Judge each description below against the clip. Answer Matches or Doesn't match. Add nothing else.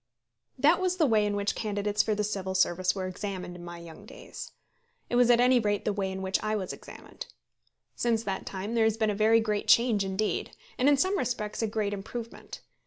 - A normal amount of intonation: Matches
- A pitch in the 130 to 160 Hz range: Doesn't match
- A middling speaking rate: Doesn't match